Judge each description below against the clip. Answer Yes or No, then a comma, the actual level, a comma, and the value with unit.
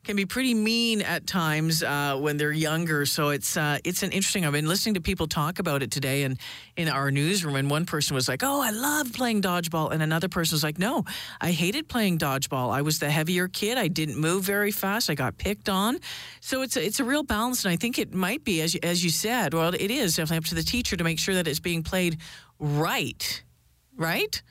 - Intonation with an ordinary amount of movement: Yes, average, 5.0 semitones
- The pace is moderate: No, fast, 240 wpm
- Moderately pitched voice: Yes, medium, 170 Hz